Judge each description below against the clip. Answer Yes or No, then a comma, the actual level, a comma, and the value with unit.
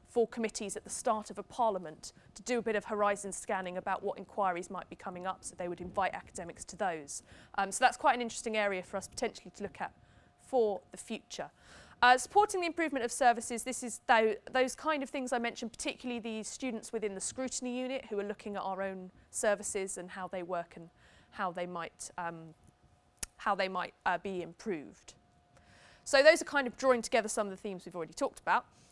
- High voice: Yes, high, 210 Hz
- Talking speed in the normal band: No, fast, 215 wpm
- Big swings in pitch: No, average, 4.7 semitones